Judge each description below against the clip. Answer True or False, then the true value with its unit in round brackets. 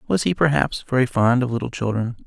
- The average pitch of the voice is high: False (120 Hz)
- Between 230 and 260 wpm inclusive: False (210 wpm)